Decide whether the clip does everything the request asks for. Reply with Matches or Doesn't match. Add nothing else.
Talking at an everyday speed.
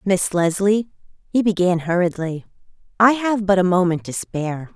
Matches